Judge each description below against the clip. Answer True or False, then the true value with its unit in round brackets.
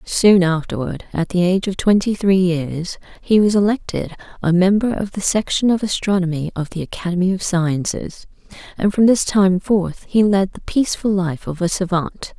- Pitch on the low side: False (185 Hz)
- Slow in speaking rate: False (180 wpm)